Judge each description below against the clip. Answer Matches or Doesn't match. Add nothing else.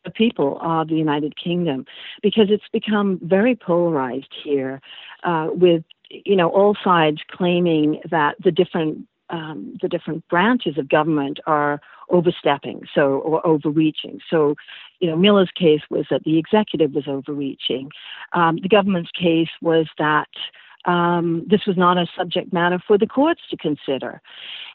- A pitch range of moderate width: Matches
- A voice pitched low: Doesn't match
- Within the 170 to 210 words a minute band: Doesn't match